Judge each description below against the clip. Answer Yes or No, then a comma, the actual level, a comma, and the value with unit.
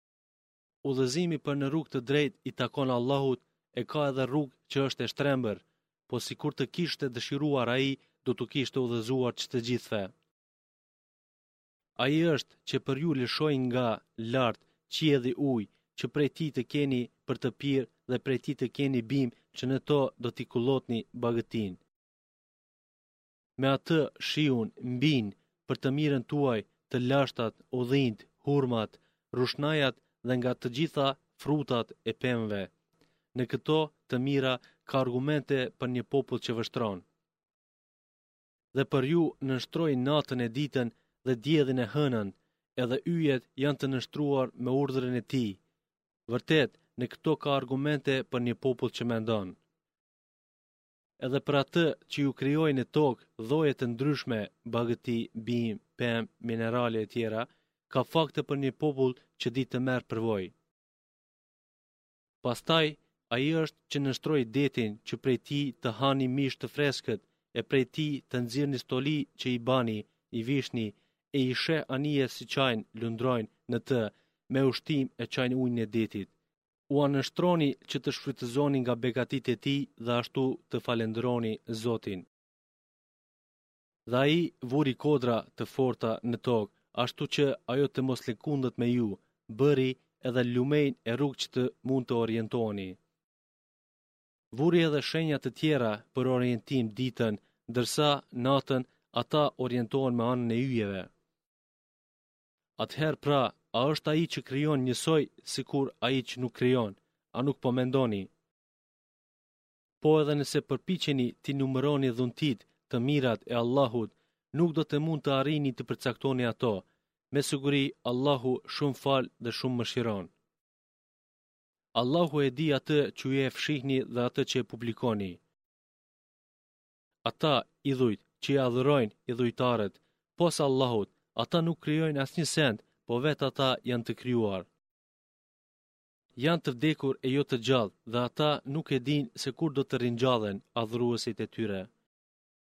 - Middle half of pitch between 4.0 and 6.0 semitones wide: No, average, 2.9 semitones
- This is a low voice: Yes, low, 130 Hz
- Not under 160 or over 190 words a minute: No, average, 150 wpm